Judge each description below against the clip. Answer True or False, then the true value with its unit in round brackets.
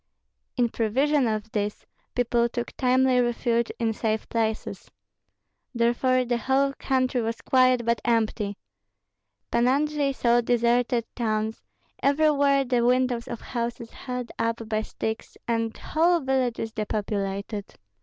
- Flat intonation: True (2.3 semitones)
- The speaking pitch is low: False (235 Hz)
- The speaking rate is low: True (125 wpm)